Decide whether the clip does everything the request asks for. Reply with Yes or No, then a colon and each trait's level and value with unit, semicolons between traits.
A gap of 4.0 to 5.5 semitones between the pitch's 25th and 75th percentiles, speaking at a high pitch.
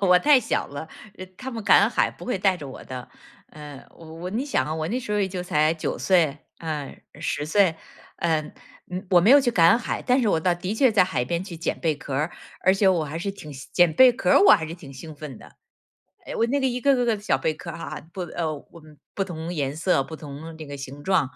No: average, 4.6 semitones; medium, 170 Hz